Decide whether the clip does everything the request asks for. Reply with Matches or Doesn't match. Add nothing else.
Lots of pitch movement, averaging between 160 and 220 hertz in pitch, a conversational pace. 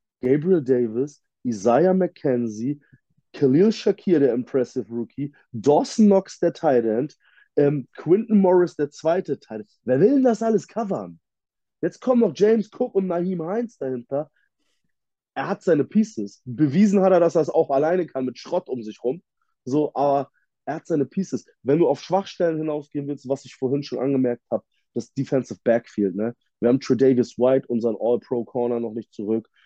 Doesn't match